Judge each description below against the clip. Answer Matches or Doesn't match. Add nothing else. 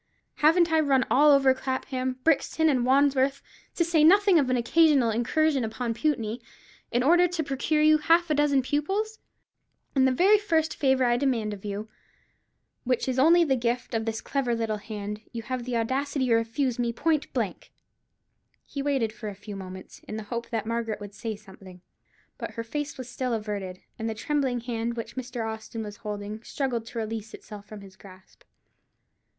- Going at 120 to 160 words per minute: Doesn't match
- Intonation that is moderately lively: Matches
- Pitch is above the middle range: Matches